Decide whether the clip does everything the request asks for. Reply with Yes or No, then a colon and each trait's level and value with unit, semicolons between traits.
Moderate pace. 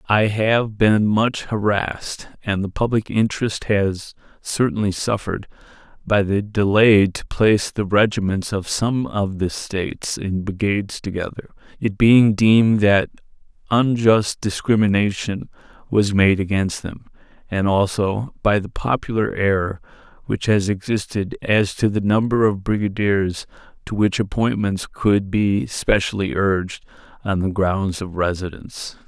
No: slow, 130 wpm